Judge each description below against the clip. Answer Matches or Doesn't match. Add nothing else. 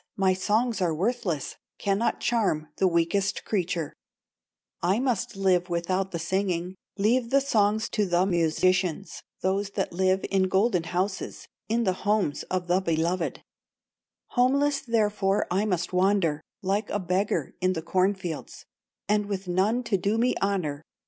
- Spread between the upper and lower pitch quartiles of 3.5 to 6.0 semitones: Doesn't match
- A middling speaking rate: Matches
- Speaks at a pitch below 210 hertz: Matches